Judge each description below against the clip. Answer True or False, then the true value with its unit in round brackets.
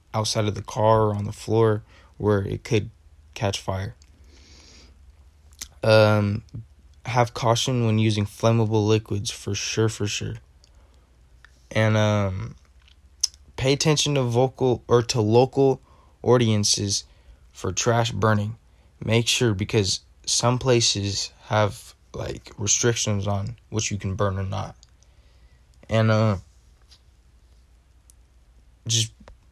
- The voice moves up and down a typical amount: False (6.8 semitones)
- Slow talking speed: True (110 wpm)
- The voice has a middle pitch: False (105 Hz)